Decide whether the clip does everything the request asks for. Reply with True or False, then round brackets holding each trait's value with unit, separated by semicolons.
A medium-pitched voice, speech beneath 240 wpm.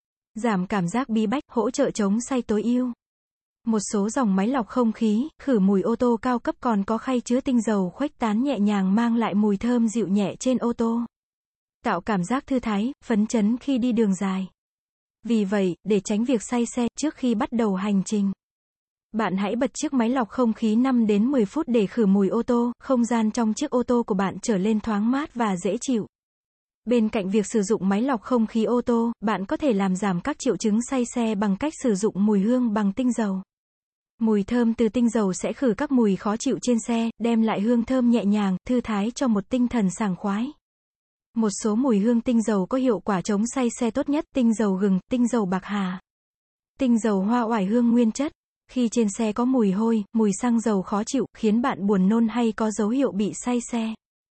False (230 Hz; 230 wpm)